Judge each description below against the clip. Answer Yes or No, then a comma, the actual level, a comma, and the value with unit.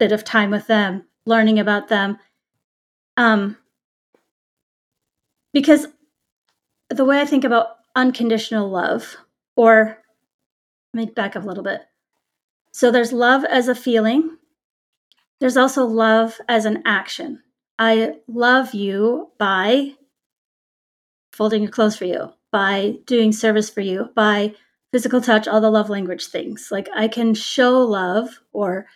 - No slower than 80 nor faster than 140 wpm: Yes, slow, 135 wpm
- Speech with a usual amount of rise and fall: Yes, average, 3.0 semitones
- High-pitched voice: Yes, high, 225 Hz